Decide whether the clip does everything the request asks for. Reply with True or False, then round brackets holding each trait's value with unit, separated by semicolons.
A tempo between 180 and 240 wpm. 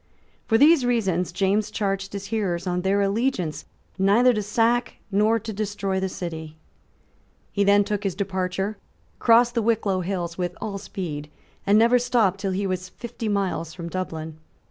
False (165 wpm)